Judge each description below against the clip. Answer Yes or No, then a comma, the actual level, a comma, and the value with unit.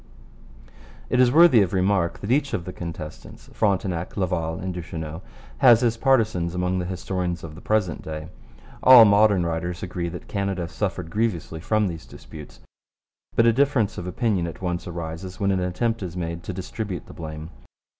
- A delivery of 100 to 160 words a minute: No, average, 175 wpm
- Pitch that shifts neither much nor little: Yes, average, 3.9 semitones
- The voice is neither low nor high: No, very low, 90 Hz